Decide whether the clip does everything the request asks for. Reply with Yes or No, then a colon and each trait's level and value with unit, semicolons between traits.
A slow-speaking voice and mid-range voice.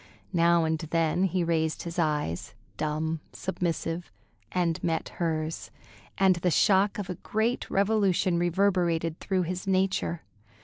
Yes: slow, 130 wpm; medium, 170 Hz